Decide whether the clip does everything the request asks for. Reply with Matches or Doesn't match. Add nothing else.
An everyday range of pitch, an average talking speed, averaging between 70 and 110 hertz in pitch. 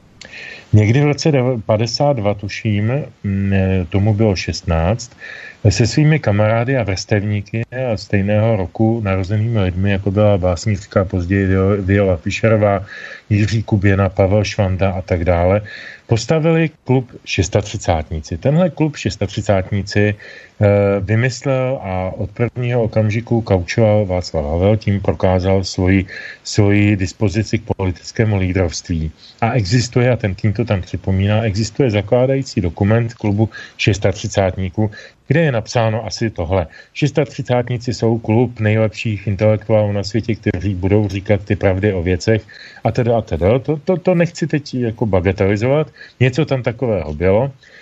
Matches